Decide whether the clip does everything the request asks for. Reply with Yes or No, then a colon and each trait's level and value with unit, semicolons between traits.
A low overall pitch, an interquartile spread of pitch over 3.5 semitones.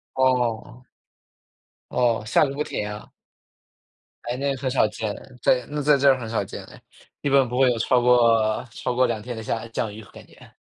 No: low, 120 Hz; average, 2.7 semitones